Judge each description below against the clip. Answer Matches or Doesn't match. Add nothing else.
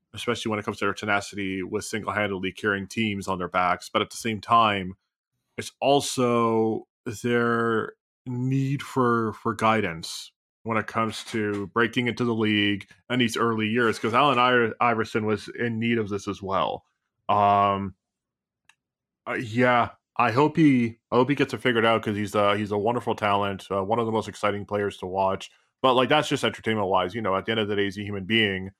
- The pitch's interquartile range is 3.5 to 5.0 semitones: Doesn't match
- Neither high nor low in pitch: Doesn't match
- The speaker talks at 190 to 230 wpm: Matches